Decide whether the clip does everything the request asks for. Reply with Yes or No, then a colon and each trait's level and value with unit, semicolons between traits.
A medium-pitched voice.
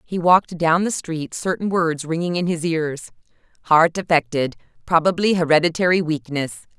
Yes: medium, 165 Hz